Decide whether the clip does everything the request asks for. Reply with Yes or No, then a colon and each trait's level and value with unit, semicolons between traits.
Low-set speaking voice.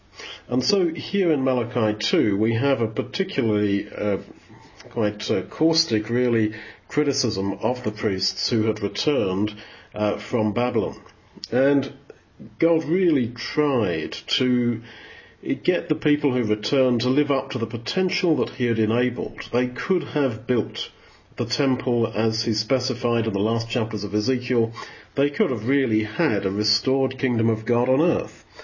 Yes: low, 120 Hz